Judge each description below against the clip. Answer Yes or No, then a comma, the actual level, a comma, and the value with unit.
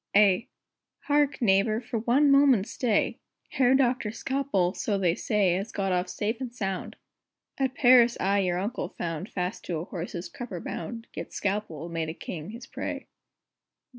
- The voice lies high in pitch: Yes, high, 210 Hz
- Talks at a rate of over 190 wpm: No, average, 165 wpm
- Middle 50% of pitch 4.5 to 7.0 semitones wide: Yes, average, 5.2 semitones